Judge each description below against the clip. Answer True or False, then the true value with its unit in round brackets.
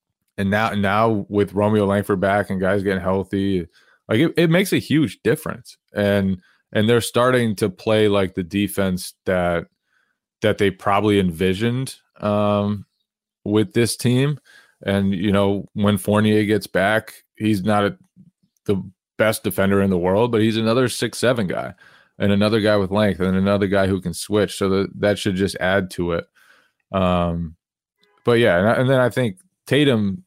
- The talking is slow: False (170 wpm)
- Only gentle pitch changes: True (2.0 semitones)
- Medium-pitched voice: False (100 Hz)